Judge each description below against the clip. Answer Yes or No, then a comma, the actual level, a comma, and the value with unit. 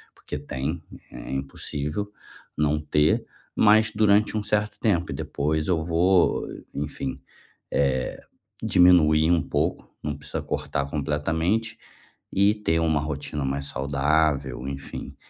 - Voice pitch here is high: No, very low, 75 Hz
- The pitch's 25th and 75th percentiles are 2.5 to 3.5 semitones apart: No, average, 4.0 semitones